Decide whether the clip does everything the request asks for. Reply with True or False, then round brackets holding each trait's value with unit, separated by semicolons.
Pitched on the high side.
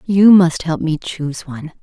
False (165 Hz)